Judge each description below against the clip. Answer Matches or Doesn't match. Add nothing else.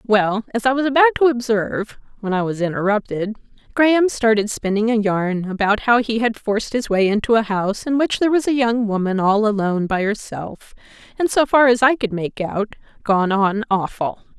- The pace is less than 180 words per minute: Doesn't match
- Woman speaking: Matches